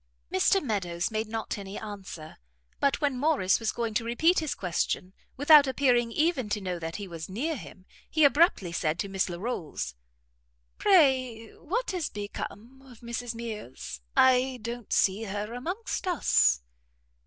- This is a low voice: No, high, 230 Hz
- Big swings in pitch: Yes, wide, 6.0 semitones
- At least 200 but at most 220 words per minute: No, average, 155 wpm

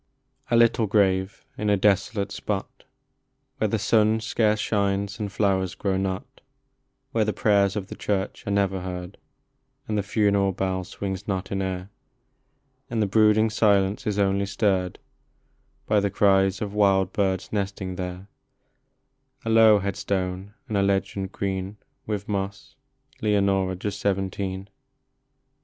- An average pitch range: No, narrow, 1.6 semitones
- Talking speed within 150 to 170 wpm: No, average, 140 wpm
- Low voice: Yes, low, 100 Hz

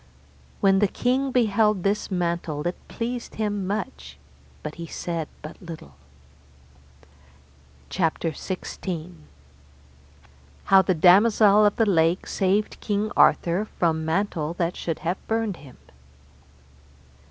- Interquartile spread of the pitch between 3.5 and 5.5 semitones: Yes, average, 4.0 semitones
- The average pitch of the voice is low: No, medium, 185 Hz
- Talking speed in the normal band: No, slow, 115 wpm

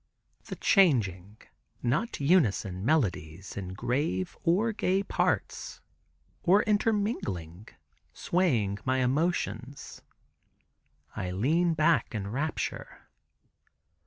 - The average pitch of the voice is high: No, low, 130 Hz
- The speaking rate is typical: No, slow, 85 wpm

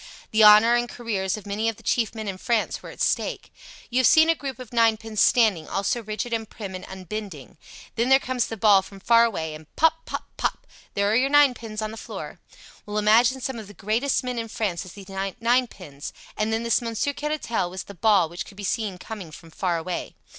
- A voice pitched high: Yes, high, 220 Hz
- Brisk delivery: Yes, fast, 225 wpm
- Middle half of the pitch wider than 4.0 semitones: No, average, 3.5 semitones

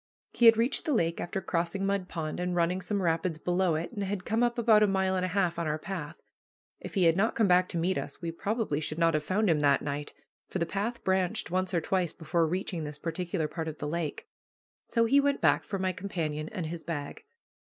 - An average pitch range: Yes, average, 3.2 semitones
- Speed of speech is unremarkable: No, fast, 240 wpm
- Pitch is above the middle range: No, medium, 180 Hz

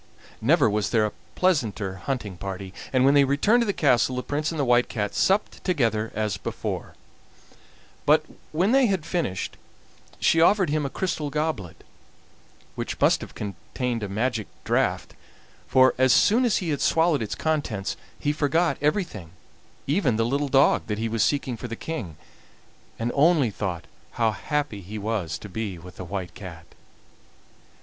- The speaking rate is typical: Yes, average, 170 wpm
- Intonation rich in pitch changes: Yes, wide, 6.6 semitones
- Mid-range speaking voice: No, low, 125 Hz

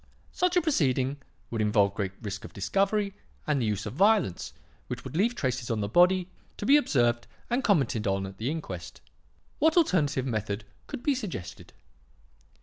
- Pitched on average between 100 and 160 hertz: Yes, low, 135 Hz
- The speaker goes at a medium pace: Yes, average, 170 wpm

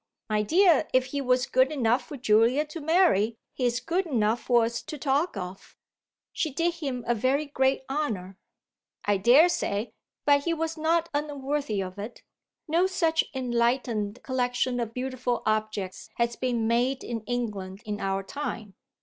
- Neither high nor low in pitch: No, very high, 250 Hz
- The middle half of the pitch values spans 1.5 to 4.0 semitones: No, average, 4.8 semitones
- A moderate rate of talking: Yes, average, 160 wpm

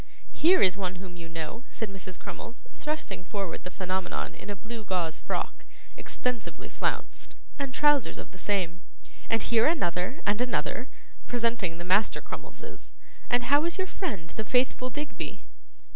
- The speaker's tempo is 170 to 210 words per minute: No, average, 160 wpm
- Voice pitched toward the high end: Yes, high, 210 Hz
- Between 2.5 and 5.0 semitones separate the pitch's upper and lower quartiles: No, wide, 5.6 semitones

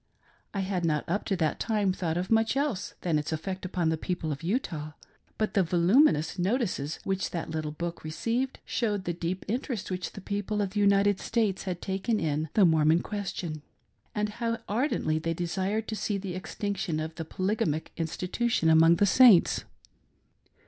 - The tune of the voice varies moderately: Yes, average, 4.3 semitones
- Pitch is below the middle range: No, medium, 185 Hz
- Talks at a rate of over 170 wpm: Yes, average, 180 wpm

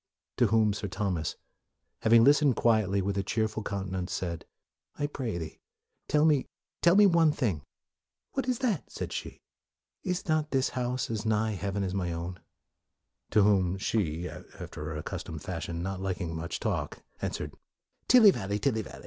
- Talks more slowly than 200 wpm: Yes, average, 180 wpm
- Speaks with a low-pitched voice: Yes, low, 105 Hz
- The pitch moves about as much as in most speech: No, wide, 6.2 semitones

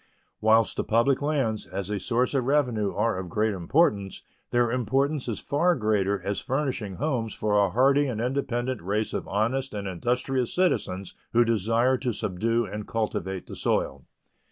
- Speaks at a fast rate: No, average, 165 wpm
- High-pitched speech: No, low, 115 Hz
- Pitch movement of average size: Yes, average, 4.1 semitones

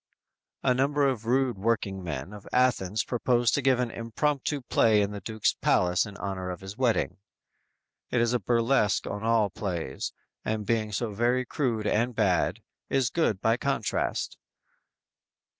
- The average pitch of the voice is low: Yes, low, 115 Hz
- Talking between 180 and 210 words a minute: No, average, 160 wpm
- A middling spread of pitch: Yes, average, 3.8 semitones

